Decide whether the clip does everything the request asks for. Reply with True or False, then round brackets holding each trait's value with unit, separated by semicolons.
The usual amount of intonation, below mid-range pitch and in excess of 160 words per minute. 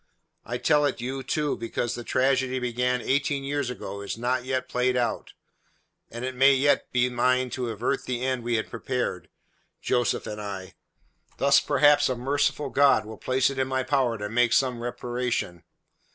False (1.9 semitones; 125 Hz; 180 wpm)